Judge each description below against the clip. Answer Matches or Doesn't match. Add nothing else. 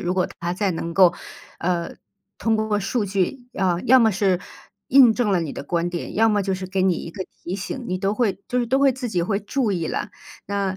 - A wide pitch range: Doesn't match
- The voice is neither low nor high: Doesn't match